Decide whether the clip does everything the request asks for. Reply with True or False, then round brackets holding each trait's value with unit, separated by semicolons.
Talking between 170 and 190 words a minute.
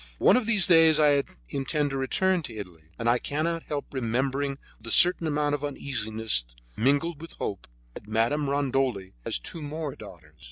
True (175 wpm)